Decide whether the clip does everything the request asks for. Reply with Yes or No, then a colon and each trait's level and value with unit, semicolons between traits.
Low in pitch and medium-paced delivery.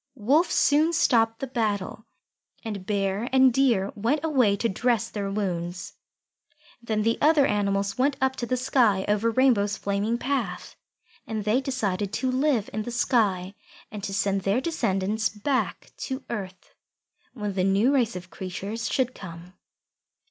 No: high, 220 Hz; average, 155 wpm